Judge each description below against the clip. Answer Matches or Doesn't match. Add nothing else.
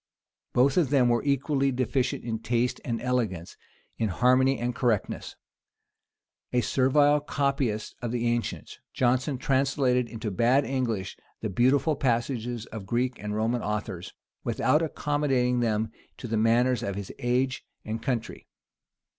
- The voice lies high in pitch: Doesn't match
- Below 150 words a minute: Matches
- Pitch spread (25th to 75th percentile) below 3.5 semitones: Matches